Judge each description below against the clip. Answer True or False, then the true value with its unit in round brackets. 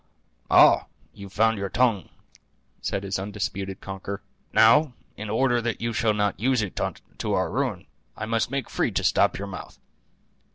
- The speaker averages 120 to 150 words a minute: False (165 wpm)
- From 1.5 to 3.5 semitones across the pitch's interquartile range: True (2.7 semitones)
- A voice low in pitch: True (105 Hz)